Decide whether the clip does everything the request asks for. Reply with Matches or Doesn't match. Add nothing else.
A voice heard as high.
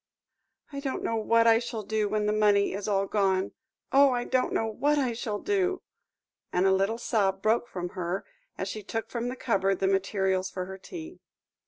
Matches